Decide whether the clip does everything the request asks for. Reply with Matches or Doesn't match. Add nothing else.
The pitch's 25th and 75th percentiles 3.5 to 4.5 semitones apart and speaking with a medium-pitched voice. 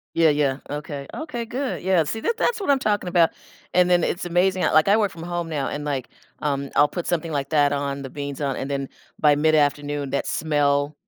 Matches